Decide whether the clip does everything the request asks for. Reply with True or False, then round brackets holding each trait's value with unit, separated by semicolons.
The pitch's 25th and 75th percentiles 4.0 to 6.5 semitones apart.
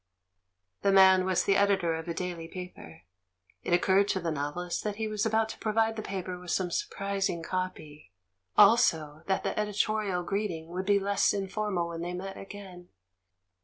False (2.7 semitones)